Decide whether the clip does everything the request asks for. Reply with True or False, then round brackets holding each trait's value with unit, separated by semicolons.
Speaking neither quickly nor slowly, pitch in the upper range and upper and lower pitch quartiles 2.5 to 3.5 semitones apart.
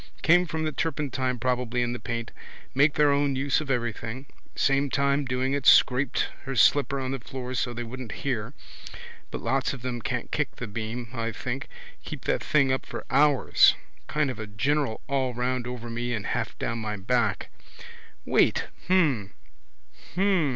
False (175 wpm; 130 Hz; 2.8 semitones)